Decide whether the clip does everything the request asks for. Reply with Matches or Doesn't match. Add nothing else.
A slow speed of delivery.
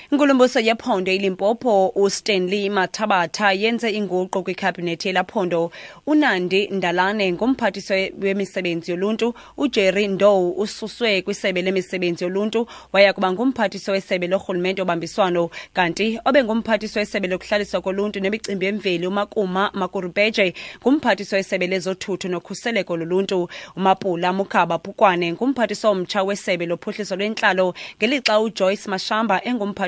Matches